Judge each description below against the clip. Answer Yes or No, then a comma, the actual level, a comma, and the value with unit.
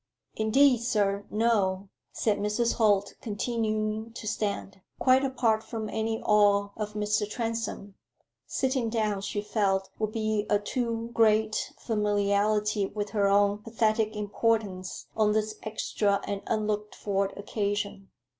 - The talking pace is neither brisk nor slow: No, slow, 125 wpm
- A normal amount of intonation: No, narrow, 1.6 semitones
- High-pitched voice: Yes, high, 210 Hz